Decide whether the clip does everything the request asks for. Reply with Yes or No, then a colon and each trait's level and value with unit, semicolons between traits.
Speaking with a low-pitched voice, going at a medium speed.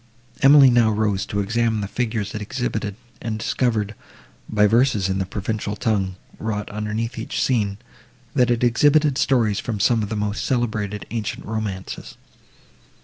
Yes: low, 110 Hz; average, 150 wpm